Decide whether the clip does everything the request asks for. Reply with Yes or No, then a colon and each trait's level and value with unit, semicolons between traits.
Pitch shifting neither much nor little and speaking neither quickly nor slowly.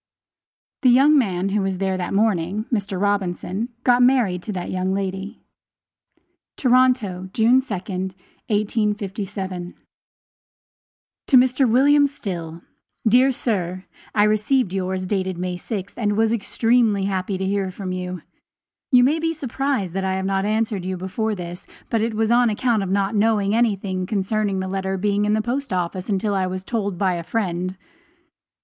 Yes: average, 3.3 semitones; average, 160 wpm